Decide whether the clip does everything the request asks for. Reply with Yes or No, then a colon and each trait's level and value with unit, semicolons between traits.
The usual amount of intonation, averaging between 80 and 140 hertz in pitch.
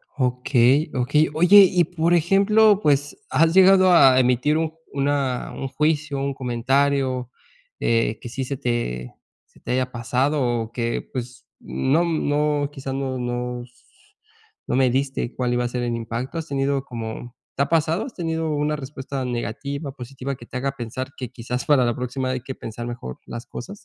Yes: average, 3.4 semitones; low, 135 Hz